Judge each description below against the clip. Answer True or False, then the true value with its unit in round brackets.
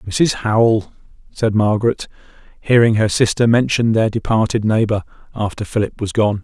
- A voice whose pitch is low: True (110 Hz)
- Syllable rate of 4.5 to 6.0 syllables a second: True (5.0 syllables/s)